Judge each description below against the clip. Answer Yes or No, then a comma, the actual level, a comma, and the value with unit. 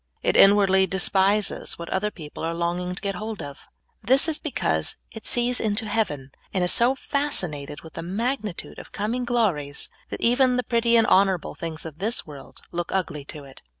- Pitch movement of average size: No, wide, 5.7 semitones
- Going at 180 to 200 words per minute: Yes, average, 190 wpm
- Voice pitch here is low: No, high, 195 Hz